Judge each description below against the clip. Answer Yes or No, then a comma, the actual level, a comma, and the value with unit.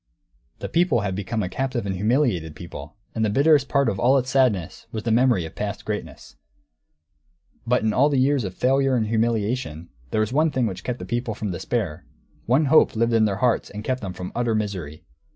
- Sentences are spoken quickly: Yes, fast, 210 wpm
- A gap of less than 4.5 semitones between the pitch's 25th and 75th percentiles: No, average, 4.8 semitones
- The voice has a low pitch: Yes, low, 115 Hz